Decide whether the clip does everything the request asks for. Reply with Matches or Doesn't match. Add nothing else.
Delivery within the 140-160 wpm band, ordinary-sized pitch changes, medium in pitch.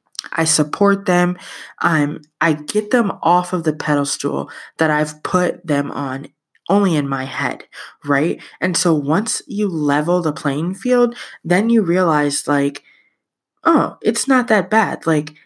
Matches